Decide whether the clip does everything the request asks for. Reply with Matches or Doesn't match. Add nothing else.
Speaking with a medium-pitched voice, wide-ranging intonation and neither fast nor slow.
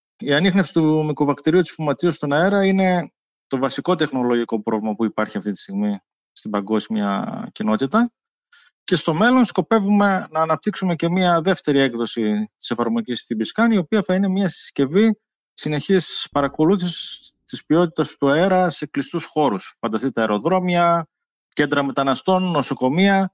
Matches